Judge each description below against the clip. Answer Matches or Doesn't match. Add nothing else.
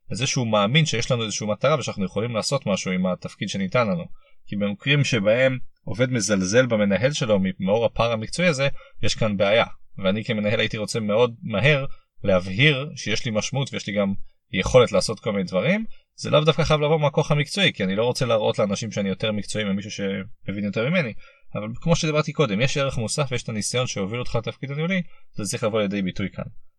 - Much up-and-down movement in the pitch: Matches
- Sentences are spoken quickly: Matches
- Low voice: Matches